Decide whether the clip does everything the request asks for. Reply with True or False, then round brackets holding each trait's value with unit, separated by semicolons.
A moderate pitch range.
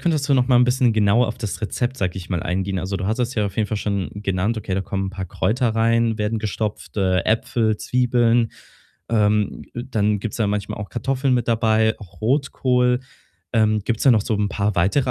True (3.1 semitones)